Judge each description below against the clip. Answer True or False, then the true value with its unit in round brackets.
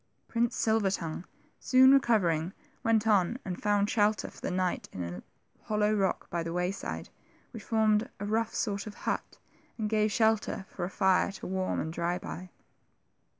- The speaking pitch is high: True (205 Hz)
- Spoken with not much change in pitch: False (3.3 semitones)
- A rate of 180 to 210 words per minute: False (170 wpm)